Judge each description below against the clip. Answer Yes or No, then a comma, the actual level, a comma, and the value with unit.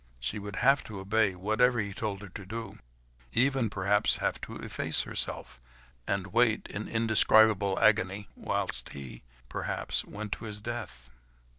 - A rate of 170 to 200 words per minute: No, average, 150 wpm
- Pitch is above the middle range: No, low, 105 Hz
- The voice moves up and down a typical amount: No, narrow, 2.3 semitones